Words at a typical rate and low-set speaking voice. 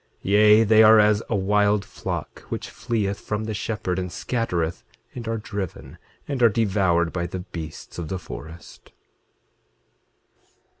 Yes: average, 150 wpm; low, 105 Hz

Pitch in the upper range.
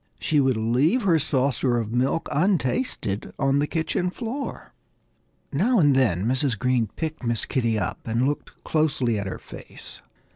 No: low, 135 Hz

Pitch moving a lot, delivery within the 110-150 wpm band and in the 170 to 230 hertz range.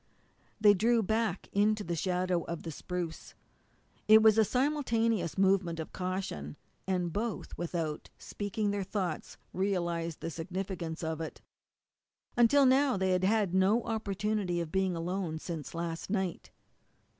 No: average, 4.0 semitones; average, 140 wpm; high, 190 Hz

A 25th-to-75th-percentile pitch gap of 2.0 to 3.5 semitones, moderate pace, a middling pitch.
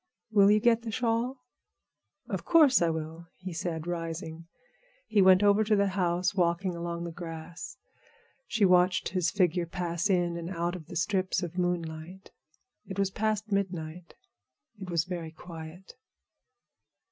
Yes: average, 2.7 semitones; average, 150 wpm; medium, 180 Hz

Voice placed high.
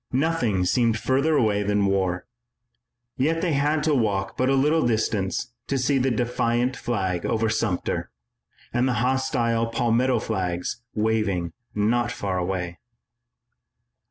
No: low, 115 Hz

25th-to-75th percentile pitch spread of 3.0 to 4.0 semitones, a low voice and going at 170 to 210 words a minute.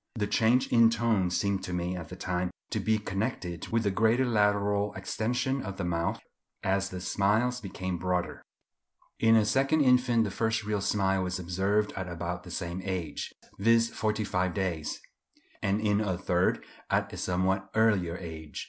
Yes: average, 3.5 semitones; low, 100 Hz; average, 175 wpm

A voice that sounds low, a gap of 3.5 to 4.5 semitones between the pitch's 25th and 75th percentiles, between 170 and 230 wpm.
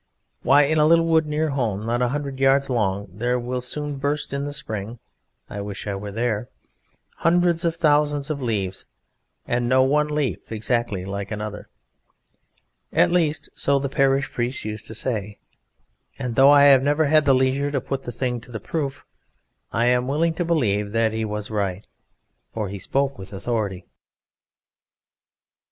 No: low, 130 Hz; average, 5.0 semitones; average, 175 wpm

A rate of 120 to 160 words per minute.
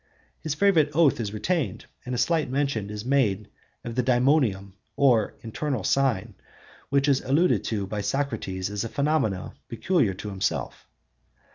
Yes: average, 150 wpm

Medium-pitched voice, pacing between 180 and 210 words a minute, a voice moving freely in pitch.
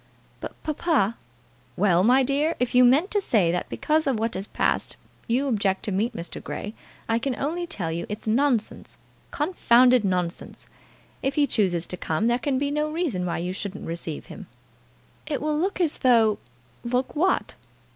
No: high, 240 Hz; average, 185 wpm; wide, 6.9 semitones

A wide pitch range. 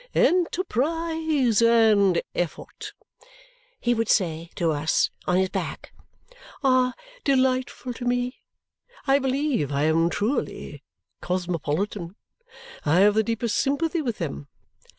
Yes: wide, 7.0 semitones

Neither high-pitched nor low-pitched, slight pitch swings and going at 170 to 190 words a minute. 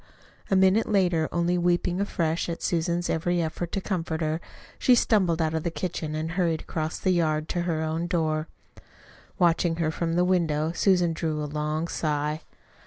Yes: medium, 165 Hz; narrow, 2.0 semitones; average, 175 wpm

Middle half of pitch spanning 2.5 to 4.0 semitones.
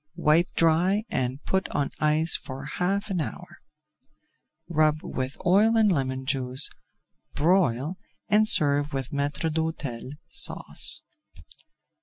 No: average, 4.7 semitones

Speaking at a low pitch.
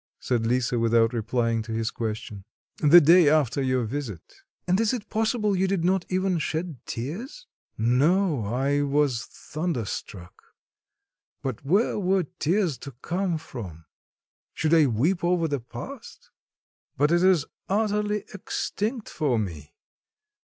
No: medium, 150 Hz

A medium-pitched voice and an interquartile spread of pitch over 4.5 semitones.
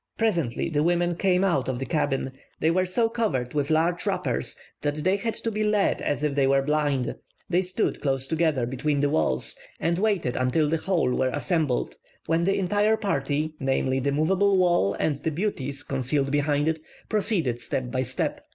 Yes: medium, 155 Hz; average, 5.2 semitones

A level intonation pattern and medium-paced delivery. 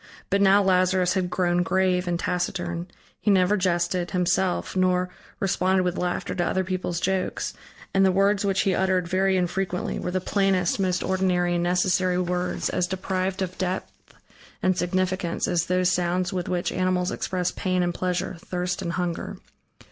Yes: narrow, 1.0 semitones; average, 165 wpm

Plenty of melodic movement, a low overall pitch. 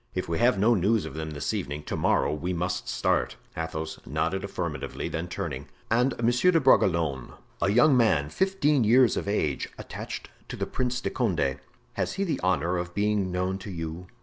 Yes: wide, 7.0 semitones; very low, 95 Hz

